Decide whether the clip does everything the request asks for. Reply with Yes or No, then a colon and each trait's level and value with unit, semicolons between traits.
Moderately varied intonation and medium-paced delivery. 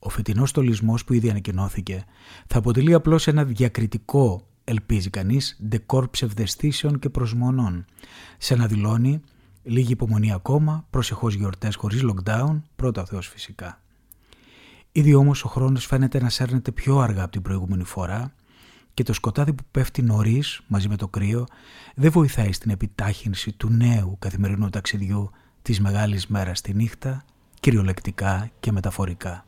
Yes: average, 4.3 semitones; average, 140 wpm